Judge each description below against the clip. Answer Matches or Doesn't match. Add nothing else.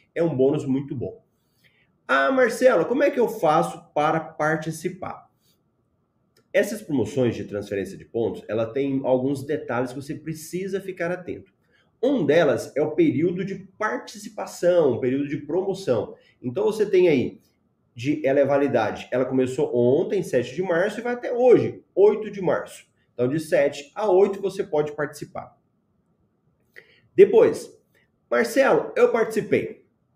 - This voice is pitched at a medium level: Matches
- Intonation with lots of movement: Matches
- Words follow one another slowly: Doesn't match